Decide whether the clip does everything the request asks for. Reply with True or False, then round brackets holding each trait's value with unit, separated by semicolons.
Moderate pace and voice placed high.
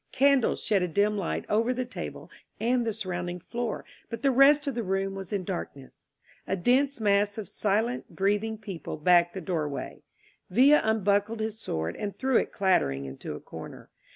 True (180 wpm; 205 Hz)